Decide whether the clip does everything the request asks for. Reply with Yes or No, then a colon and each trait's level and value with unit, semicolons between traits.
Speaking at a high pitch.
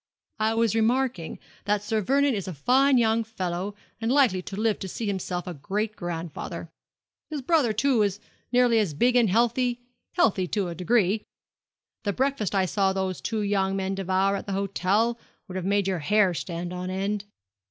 Yes: high, 205 Hz